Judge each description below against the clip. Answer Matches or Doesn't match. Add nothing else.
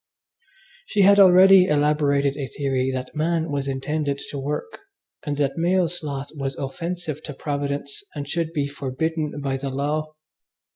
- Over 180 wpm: Doesn't match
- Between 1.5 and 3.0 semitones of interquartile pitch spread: Matches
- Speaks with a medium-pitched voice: Matches